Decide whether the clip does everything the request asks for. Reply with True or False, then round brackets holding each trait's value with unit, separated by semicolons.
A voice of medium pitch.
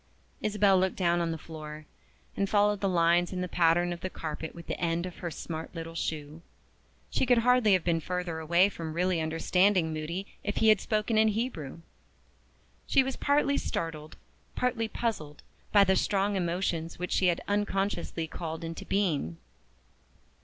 True (175 Hz)